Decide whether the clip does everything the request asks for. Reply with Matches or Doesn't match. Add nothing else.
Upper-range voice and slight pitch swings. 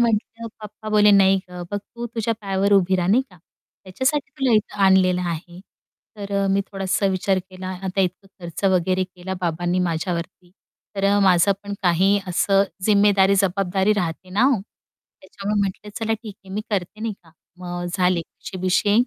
Matches